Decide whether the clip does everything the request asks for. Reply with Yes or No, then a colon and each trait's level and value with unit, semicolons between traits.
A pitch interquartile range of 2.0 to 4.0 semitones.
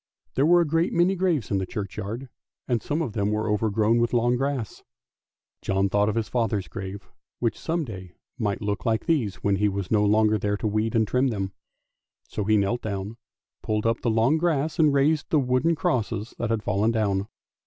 No: average, 4.7 semitones